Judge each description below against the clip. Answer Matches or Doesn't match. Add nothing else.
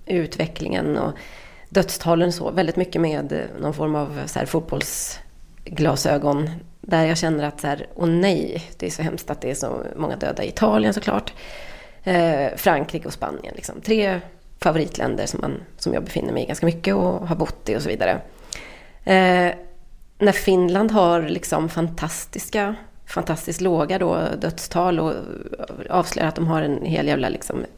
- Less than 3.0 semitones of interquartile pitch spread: Matches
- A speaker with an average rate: Matches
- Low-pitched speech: Doesn't match